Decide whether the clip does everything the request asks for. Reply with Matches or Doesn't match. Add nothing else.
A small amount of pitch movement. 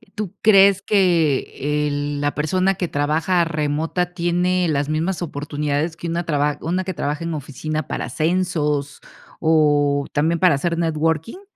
Doesn't match